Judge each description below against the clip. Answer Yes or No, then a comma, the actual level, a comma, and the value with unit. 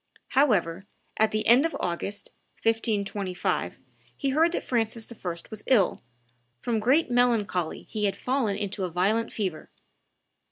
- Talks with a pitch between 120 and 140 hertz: No, high, 215 Hz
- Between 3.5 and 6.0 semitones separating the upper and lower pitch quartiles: Yes, average, 3.8 semitones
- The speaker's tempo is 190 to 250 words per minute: No, slow, 135 wpm